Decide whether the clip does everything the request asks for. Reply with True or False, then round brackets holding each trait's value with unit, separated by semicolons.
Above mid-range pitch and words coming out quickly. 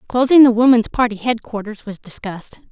False (230 Hz; 155 wpm)